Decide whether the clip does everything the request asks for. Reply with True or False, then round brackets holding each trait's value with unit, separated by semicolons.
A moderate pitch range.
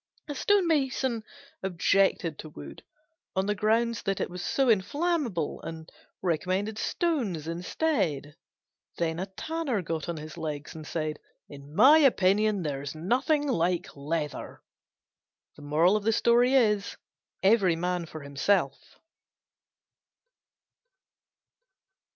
False (6.6 semitones)